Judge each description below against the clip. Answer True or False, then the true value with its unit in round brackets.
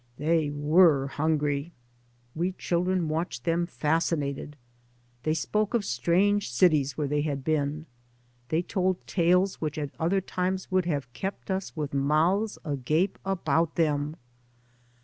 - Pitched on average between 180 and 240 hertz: False (160 Hz)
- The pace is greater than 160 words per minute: False (135 wpm)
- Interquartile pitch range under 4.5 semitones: True (3.7 semitones)